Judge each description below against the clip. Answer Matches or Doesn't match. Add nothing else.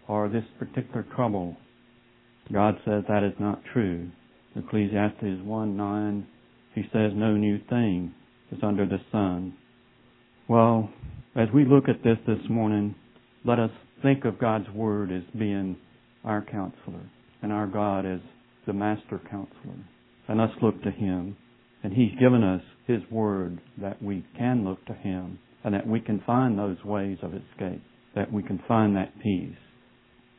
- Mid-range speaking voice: Doesn't match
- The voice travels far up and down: Doesn't match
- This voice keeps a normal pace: Matches